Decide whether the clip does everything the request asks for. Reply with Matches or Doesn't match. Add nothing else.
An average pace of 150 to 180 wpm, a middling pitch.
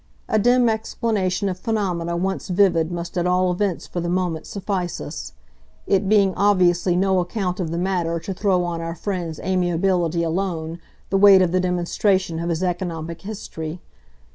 Matches